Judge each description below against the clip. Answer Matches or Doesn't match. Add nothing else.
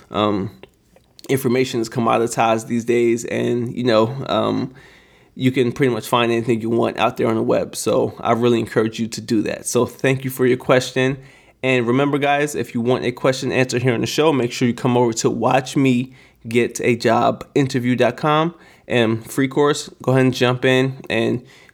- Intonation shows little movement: Matches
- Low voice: Matches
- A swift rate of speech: Matches